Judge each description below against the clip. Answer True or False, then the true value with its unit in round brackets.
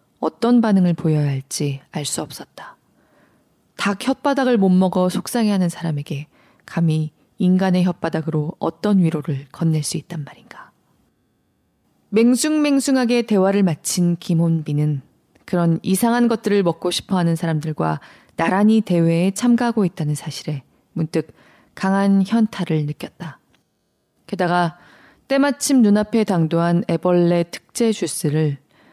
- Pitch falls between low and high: True (175 Hz)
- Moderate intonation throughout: True (4.5 semitones)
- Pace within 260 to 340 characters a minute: True (280 characters per minute)